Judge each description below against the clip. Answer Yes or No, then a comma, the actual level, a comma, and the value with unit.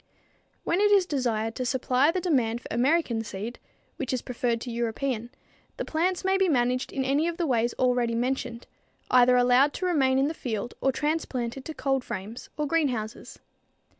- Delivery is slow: No, average, 180 wpm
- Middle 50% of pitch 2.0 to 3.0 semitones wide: No, average, 4.1 semitones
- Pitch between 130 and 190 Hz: No, very high, 255 Hz